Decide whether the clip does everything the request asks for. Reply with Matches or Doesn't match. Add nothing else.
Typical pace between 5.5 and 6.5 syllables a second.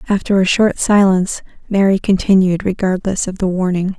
Doesn't match